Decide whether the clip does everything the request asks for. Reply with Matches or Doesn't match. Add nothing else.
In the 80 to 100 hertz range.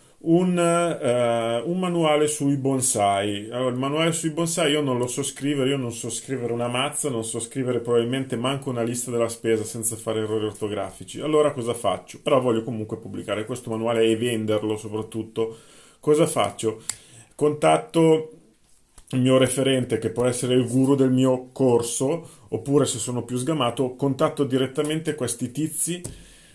Doesn't match